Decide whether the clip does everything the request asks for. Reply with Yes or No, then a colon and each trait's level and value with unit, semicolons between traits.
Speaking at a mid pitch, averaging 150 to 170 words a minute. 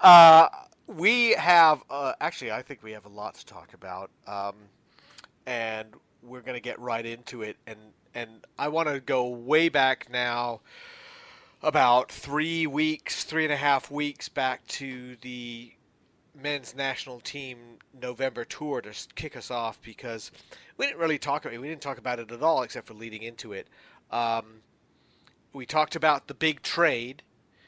No: low, 125 Hz; average, 165 wpm